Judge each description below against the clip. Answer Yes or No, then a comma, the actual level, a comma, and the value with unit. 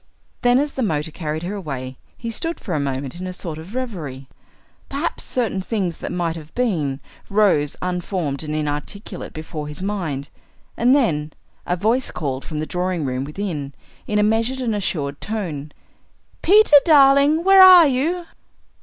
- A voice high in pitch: No, medium, 180 Hz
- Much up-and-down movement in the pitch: Yes, wide, 8.3 semitones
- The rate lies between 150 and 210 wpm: Yes, average, 165 wpm